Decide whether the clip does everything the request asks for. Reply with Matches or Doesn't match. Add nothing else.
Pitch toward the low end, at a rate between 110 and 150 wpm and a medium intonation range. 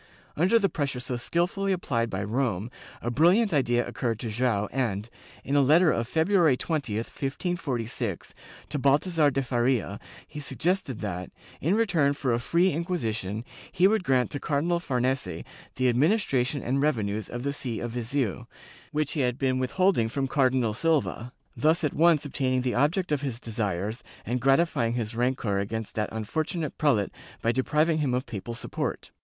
Doesn't match